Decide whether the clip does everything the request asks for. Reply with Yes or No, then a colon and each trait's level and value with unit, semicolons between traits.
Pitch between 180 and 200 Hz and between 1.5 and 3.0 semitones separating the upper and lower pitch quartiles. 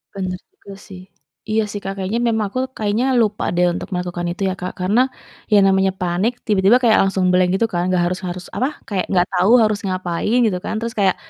Yes: high, 190 Hz; average, 2.7 semitones